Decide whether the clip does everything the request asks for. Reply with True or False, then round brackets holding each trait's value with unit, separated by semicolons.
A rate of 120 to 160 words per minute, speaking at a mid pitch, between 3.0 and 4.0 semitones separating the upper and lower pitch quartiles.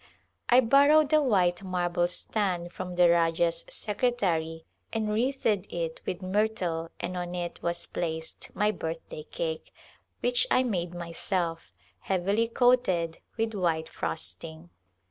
False (135 wpm; 180 Hz; 4.7 semitones)